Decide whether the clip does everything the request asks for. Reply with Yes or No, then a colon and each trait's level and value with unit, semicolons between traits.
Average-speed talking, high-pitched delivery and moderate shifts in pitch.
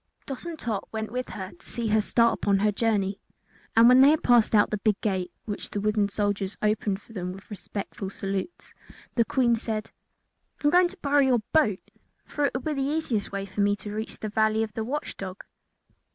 No: fast, 225 wpm; high, 215 Hz; average, 3.6 semitones